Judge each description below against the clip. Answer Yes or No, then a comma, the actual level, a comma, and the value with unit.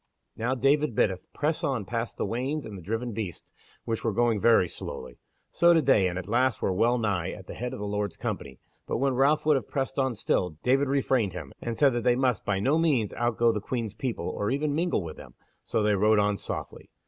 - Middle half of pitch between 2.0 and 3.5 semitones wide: No, average, 4.6 semitones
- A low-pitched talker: Yes, low, 115 Hz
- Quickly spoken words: Yes, fast, 230 wpm